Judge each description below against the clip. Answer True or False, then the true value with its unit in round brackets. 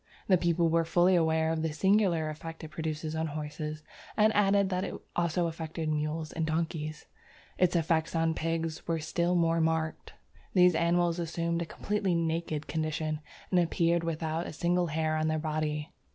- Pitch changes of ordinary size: False (1.5 semitones)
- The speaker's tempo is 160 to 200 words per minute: True (170 wpm)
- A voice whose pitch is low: False (165 Hz)